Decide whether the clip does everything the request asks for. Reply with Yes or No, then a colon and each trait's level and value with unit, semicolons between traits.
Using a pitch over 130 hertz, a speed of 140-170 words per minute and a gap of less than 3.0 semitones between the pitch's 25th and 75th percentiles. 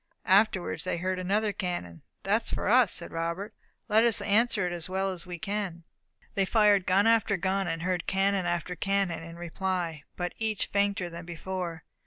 No: medium, 185 Hz; average, 185 wpm; narrow, 2.5 semitones